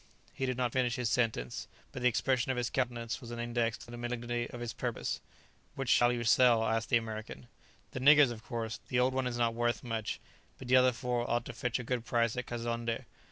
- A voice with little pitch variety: Yes, narrow, 1.2 semitones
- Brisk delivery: Yes, fast, 230 wpm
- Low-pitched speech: Yes, low, 120 Hz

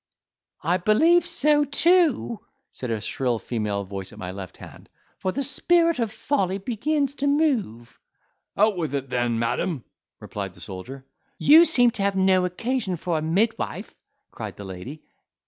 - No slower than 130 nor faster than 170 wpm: Yes, average, 160 wpm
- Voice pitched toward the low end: No, medium, 185 Hz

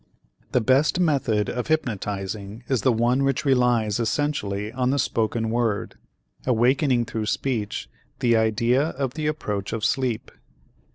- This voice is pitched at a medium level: No, low, 120 Hz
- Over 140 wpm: No, slow, 135 wpm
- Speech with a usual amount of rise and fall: Yes, average, 3.5 semitones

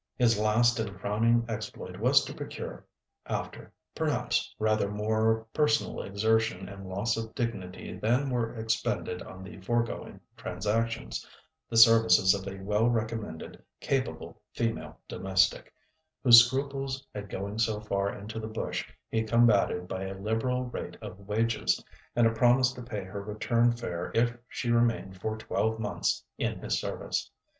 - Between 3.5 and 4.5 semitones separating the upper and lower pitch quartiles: No, average, 2.7 semitones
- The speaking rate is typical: Yes, average, 150 wpm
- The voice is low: Yes, low, 110 Hz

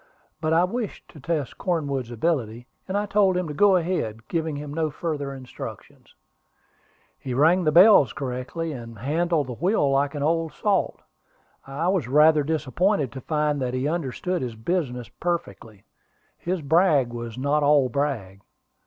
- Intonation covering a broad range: No, average, 4.8 semitones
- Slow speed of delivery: No, average, 160 wpm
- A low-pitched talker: No, medium, 150 Hz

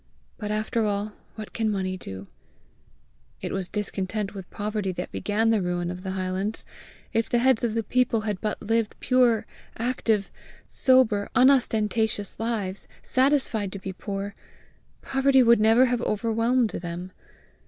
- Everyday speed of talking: Yes, average, 145 wpm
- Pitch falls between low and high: No, high, 215 Hz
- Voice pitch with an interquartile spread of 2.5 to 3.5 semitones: Yes, average, 3.0 semitones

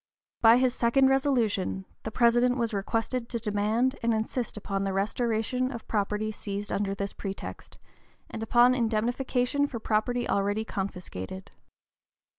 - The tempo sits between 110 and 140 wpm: Yes, slow, 135 wpm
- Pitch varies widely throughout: No, average, 3.2 semitones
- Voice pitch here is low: No, high, 225 Hz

